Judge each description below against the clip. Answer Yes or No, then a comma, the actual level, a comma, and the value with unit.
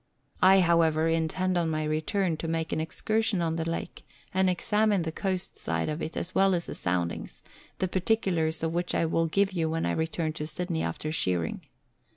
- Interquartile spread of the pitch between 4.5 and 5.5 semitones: No, average, 2.7 semitones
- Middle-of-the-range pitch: Yes, medium, 165 Hz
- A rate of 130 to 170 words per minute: No, average, 195 wpm